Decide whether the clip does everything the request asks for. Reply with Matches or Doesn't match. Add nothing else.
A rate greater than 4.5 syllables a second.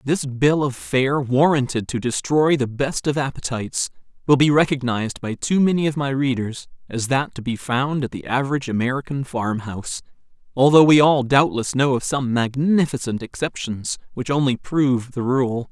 Matches